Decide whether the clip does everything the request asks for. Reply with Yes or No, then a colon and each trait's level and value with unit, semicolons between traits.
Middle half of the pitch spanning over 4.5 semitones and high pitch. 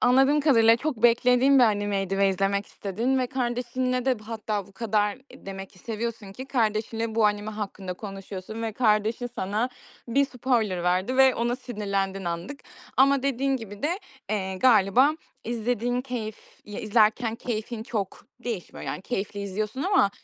No: average, 3.8 semitones; high, 225 Hz